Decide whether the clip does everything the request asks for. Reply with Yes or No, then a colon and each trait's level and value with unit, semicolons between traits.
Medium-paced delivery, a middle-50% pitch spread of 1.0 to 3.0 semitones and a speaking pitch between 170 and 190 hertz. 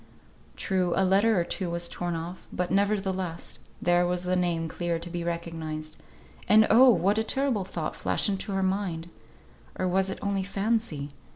Yes: average, 170 wpm; narrow, 2.6 semitones; medium, 185 Hz